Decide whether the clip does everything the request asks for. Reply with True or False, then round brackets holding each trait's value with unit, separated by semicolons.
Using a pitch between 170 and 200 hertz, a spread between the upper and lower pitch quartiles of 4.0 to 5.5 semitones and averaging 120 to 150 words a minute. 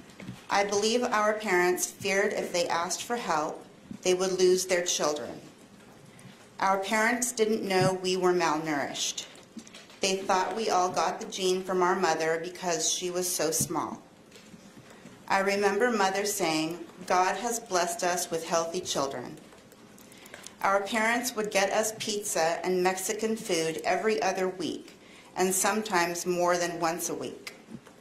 False (185 Hz; 2.8 semitones; 145 wpm)